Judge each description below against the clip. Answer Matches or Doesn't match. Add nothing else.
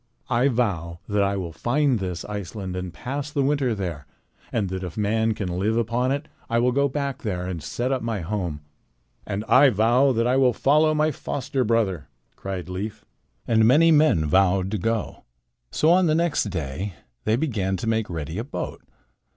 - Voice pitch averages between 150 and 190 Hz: Doesn't match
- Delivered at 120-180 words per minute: Doesn't match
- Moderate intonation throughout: Doesn't match